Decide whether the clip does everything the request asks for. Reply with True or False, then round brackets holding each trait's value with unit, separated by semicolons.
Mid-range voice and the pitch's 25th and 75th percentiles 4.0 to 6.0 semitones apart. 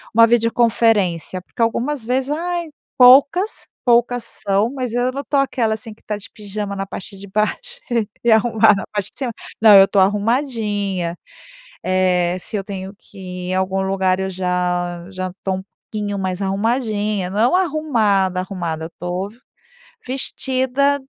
False (210 Hz; 4.5 semitones)